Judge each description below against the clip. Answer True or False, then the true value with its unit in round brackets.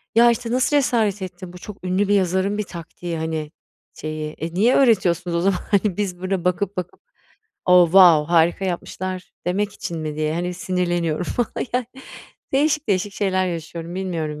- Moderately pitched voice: True (180 Hz)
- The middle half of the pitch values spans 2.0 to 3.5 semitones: True (3.0 semitones)